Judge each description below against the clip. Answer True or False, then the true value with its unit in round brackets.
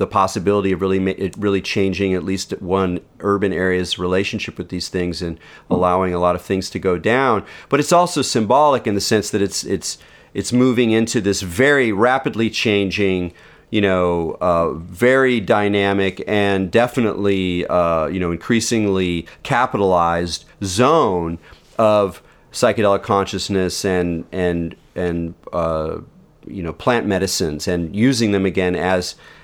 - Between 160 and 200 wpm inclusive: False (145 wpm)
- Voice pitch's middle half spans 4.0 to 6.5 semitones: False (3.0 semitones)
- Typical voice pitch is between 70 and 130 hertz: True (95 Hz)